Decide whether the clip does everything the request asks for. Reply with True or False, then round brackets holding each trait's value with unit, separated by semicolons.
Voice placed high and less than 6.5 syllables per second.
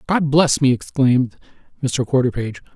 False (135 Hz; 5.3 syllables/s)